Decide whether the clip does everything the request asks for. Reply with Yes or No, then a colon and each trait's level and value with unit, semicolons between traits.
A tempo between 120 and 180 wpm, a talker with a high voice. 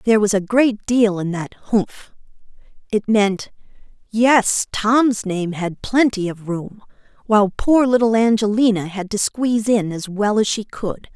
Yes: average, 160 wpm; high, 215 Hz